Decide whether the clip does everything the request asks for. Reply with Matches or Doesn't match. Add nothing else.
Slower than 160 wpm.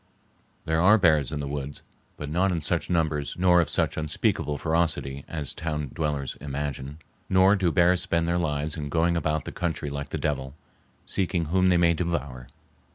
Doesn't match